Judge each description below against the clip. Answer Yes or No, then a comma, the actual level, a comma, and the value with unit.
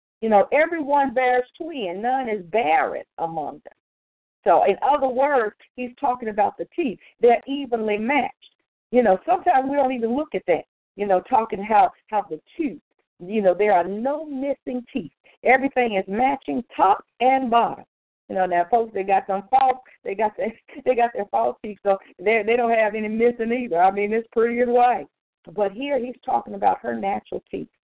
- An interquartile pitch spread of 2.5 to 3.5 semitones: No, average, 4.2 semitones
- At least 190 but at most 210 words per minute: Yes, average, 195 wpm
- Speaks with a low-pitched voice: No, high, 240 Hz